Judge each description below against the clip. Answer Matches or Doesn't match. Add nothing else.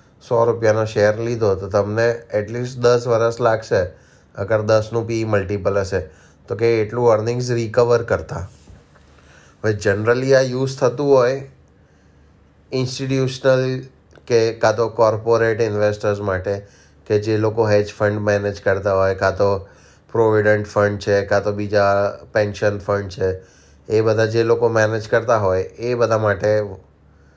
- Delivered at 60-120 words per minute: Doesn't match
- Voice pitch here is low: Matches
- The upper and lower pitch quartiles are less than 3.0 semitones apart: Matches